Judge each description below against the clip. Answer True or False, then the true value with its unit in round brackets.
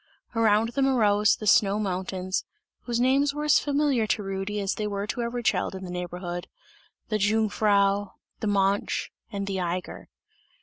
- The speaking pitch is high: True (205 Hz)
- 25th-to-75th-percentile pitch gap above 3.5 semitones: False (2.9 semitones)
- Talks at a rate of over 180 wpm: False (165 wpm)